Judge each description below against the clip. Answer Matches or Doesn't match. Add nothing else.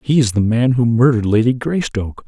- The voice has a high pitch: Doesn't match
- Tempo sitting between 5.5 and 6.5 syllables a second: Matches